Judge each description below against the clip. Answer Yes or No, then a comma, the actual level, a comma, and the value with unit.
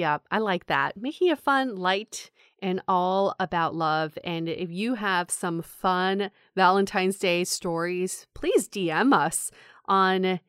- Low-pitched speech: No, medium, 185 Hz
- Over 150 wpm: No, average, 145 wpm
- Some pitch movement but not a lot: No, narrow, 2.1 semitones